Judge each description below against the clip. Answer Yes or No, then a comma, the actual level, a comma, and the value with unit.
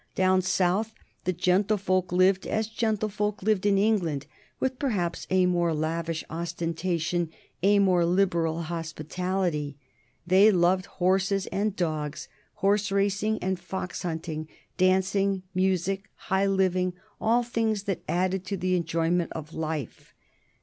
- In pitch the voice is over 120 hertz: Yes, medium, 185 Hz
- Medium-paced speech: No, slow, 125 wpm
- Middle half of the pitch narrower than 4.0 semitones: Yes, narrow, 2.5 semitones